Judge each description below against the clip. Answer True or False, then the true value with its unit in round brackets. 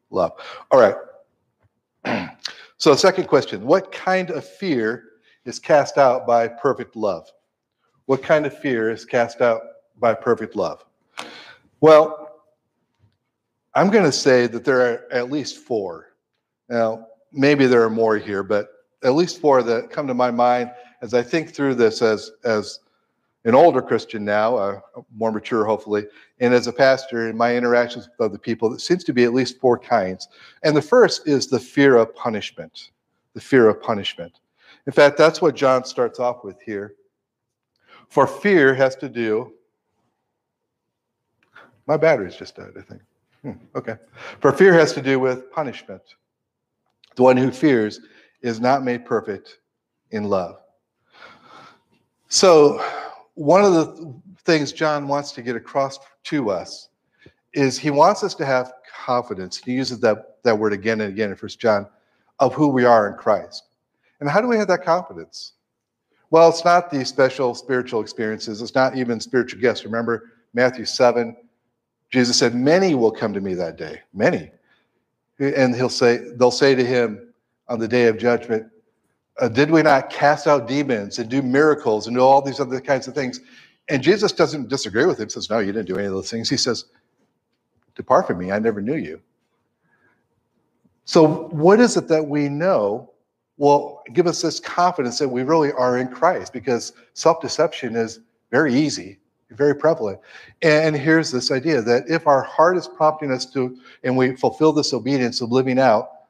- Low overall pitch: True (130 Hz)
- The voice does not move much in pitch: False (4.0 semitones)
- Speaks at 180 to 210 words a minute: False (170 wpm)